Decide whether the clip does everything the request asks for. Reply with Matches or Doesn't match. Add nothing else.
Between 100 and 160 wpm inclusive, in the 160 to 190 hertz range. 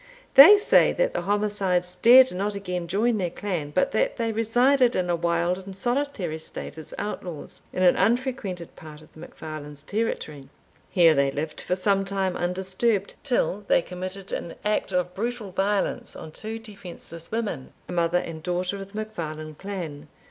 Doesn't match